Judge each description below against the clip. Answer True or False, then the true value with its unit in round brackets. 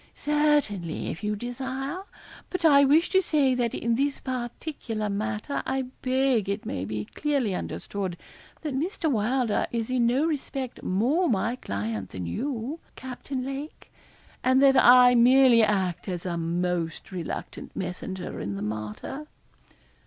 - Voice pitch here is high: True (245 Hz)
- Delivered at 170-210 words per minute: False (145 wpm)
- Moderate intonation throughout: False (6.3 semitones)